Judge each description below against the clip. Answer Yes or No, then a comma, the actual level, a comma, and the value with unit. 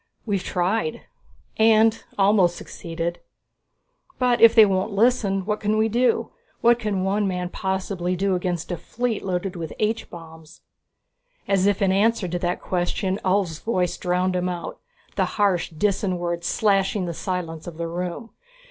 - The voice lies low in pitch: No, high, 190 Hz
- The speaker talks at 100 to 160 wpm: Yes, average, 155 wpm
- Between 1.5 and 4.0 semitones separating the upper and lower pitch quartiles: Yes, average, 3.1 semitones